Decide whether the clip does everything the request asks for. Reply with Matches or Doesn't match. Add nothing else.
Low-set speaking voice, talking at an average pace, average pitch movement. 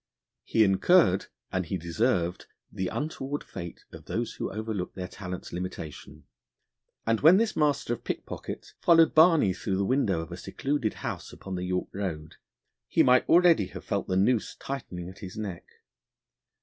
Doesn't match